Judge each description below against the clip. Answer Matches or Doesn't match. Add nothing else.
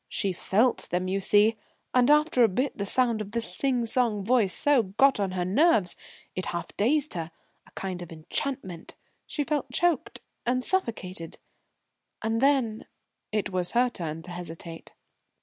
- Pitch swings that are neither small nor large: Doesn't match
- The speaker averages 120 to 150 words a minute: Doesn't match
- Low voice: Doesn't match